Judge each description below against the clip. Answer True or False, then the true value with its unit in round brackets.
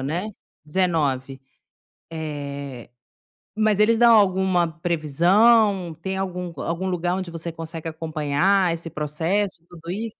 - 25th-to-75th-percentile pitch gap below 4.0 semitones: True (2.9 semitones)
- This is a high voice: False (175 Hz)